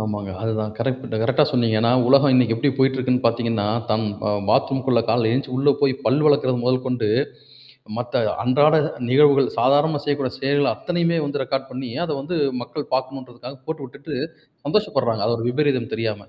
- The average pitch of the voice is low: Yes, low, 130 Hz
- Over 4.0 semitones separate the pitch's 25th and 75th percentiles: No, average, 3.3 semitones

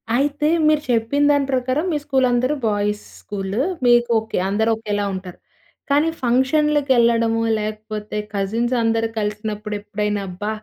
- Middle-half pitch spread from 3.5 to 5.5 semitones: Yes, average, 4.0 semitones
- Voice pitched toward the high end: Yes, high, 225 Hz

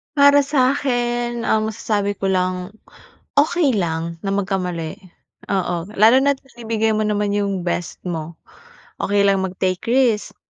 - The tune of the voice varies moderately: Yes, average, 4.6 semitones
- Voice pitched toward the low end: No, high, 205 Hz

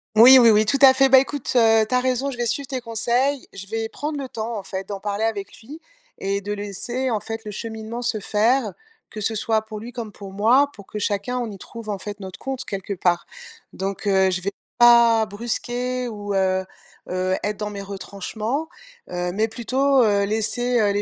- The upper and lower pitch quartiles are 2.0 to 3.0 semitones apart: No, average, 3.4 semitones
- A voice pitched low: No, high, 220 Hz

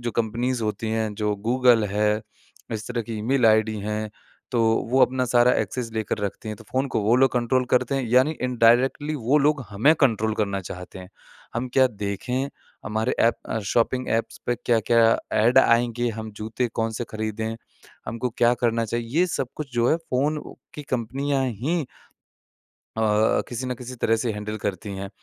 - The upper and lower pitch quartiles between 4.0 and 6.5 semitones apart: No, average, 2.8 semitones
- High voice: No, low, 115 Hz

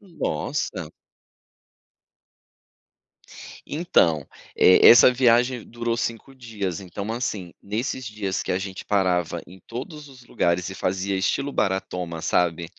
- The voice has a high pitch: No, low, 100 Hz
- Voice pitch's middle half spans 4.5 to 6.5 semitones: Yes, average, 4.9 semitones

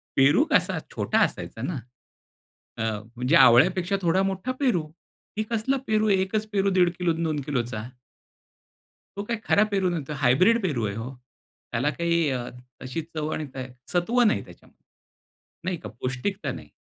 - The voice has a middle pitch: Yes, medium, 175 Hz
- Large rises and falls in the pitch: Yes, wide, 6.7 semitones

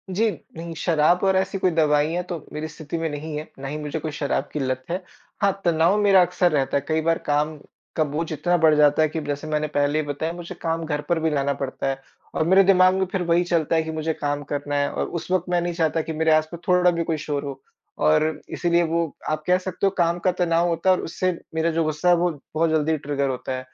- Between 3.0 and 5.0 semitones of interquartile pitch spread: No, narrow, 2.6 semitones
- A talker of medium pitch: Yes, medium, 160 Hz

